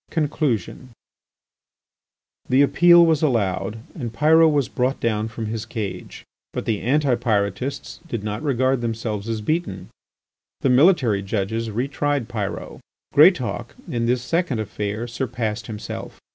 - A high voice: No, low, 120 Hz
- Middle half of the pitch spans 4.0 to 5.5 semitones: Yes, average, 4.5 semitones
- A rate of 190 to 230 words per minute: No, slow, 135 wpm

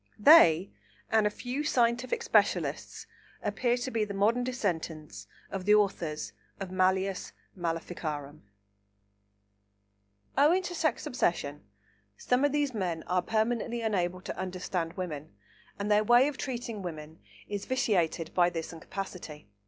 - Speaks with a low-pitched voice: No, high, 195 Hz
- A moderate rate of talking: No, slow, 130 wpm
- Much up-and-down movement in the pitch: Yes, wide, 6.0 semitones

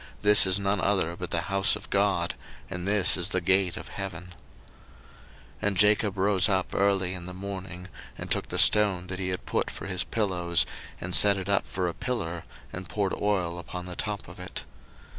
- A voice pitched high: No, very low, 95 Hz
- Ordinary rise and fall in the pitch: No, narrow, 2.0 semitones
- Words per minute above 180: Yes, average, 200 wpm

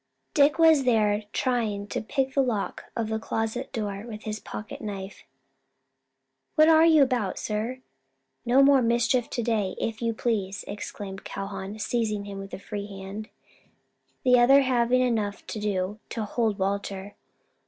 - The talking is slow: No, average, 155 wpm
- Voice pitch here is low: No, high, 220 Hz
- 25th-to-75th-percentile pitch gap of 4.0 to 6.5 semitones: No, average, 3.6 semitones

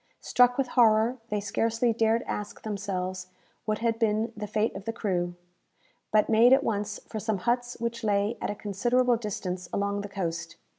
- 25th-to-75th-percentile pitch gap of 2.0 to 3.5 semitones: Yes, narrow, 2.6 semitones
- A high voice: Yes, high, 215 Hz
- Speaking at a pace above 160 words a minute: Yes, average, 180 wpm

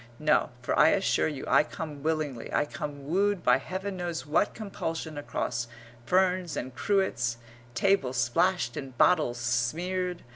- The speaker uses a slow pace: No, average, 145 wpm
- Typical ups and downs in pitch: No, wide, 6.0 semitones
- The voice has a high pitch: No, medium, 155 Hz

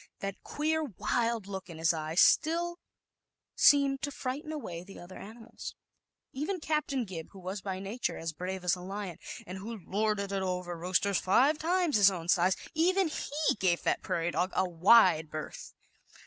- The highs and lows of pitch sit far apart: Yes, wide, 7.5 semitones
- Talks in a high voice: Yes, high, 200 Hz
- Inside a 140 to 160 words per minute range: No, average, 175 wpm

